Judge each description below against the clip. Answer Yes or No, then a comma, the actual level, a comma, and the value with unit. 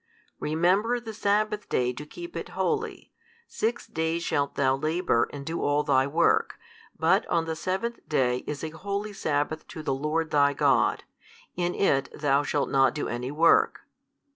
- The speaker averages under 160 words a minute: No, average, 165 wpm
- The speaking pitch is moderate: Yes, medium, 155 Hz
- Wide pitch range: No, average, 5.0 semitones